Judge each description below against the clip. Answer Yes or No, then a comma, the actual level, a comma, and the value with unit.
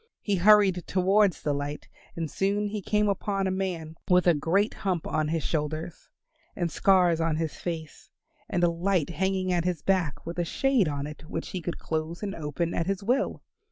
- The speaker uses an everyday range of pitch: Yes, average, 3.4 semitones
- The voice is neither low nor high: Yes, medium, 175 Hz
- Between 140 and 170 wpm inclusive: No, average, 195 wpm